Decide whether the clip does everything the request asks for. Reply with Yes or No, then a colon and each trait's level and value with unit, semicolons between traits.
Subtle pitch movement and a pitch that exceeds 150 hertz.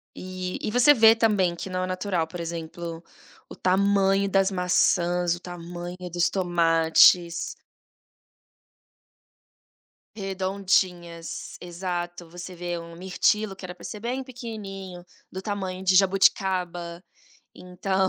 Yes: narrow, 2.0 semitones; medium, 185 Hz